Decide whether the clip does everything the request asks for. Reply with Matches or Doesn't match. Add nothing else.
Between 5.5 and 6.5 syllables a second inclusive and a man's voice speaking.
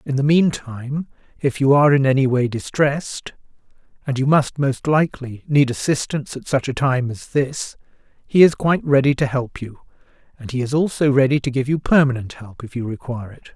Matches